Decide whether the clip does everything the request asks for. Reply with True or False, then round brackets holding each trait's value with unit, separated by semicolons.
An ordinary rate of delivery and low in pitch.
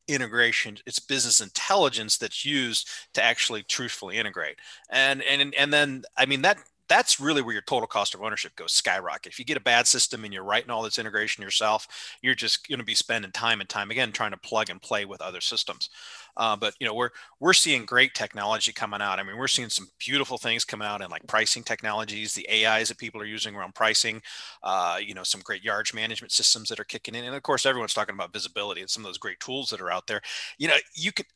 False (235 wpm; 115 Hz)